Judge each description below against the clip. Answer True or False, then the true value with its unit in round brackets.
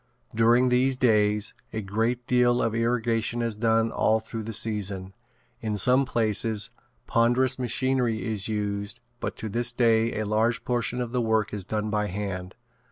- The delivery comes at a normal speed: True (160 wpm)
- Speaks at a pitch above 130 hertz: False (115 Hz)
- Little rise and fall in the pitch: True (2.3 semitones)